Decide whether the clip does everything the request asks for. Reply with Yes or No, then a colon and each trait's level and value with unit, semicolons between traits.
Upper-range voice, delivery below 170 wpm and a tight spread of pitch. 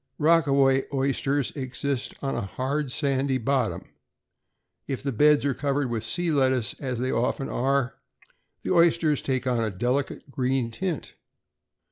No: low, 135 Hz; average, 140 wpm; narrow, 2.1 semitones